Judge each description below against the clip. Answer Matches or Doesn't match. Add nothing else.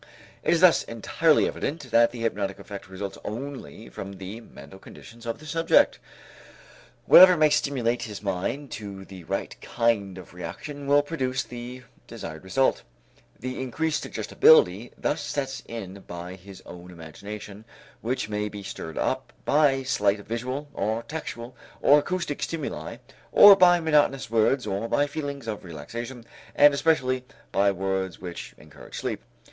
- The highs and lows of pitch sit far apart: Matches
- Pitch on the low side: Matches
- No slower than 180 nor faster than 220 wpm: Doesn't match